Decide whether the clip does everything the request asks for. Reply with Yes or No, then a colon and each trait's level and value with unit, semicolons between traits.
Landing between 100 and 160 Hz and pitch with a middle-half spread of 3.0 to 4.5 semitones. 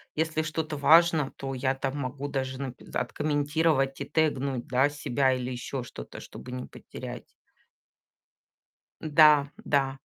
No: medium, 140 Hz; narrow, 2.5 semitones